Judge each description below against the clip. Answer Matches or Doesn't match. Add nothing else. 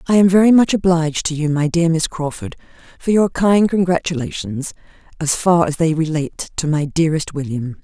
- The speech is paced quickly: Doesn't match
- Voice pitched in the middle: Matches